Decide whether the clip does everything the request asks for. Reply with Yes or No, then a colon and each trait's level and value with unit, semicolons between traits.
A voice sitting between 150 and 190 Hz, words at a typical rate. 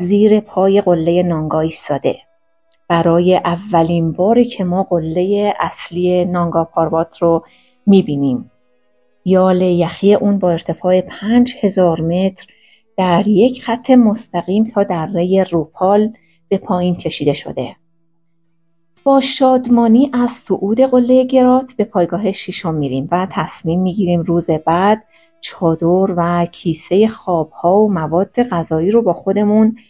Yes: medium, 185 Hz; average, 120 wpm